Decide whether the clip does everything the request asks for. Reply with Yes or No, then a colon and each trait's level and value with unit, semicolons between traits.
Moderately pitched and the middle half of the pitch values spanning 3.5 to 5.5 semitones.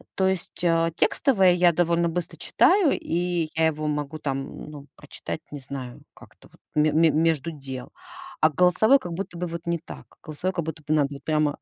No: medium, 165 Hz; average, 2.8 semitones